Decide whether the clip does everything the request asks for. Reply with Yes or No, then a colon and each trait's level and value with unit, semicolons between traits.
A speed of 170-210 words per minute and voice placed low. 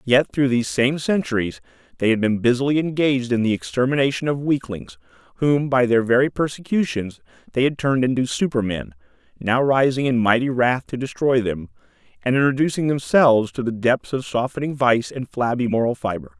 Yes: average, 175 wpm; low, 125 Hz